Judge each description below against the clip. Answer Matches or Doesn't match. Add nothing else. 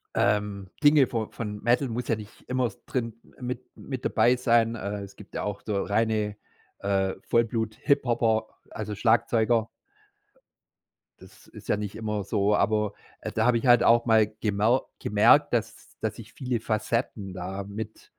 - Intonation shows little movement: Matches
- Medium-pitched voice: Doesn't match